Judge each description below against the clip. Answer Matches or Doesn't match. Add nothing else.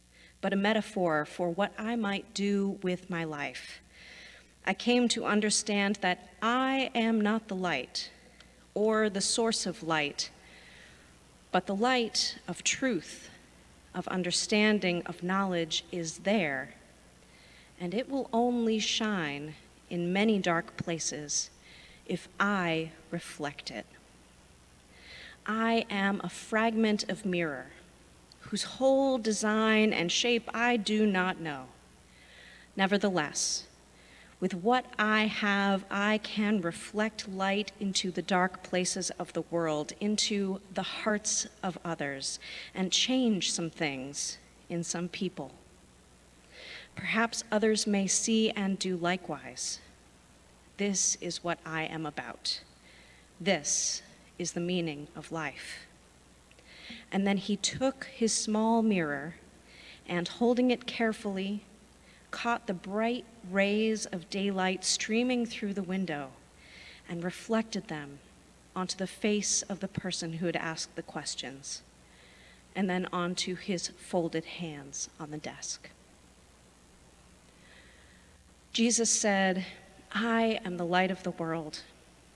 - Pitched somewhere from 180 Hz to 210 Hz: Matches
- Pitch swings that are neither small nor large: Matches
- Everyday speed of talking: Doesn't match